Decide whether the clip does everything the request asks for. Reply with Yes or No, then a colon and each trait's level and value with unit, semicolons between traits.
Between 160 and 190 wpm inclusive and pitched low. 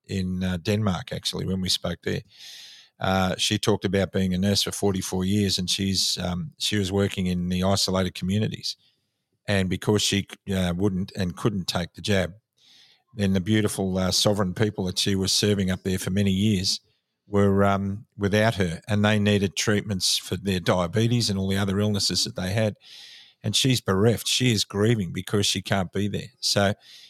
Yes: average, 185 wpm; low, 100 Hz